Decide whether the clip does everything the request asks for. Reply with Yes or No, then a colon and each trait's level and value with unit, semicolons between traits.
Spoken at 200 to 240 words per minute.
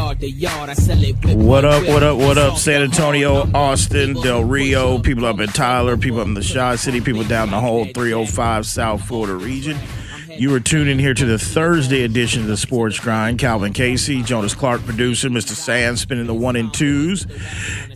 No: average, 175 wpm